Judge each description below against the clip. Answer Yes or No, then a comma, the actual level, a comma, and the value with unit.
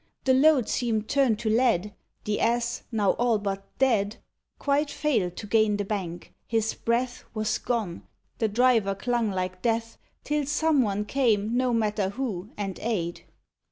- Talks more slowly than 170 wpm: Yes, average, 160 wpm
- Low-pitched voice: No, high, 225 Hz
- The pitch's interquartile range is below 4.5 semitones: Yes, average, 3.3 semitones